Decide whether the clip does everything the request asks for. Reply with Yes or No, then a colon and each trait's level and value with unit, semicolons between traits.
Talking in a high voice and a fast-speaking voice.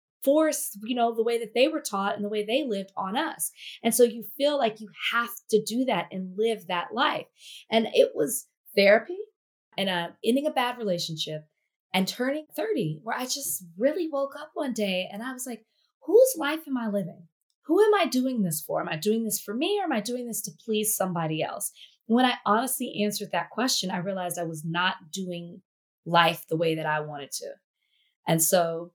Yes: high, 215 Hz; fast, 215 wpm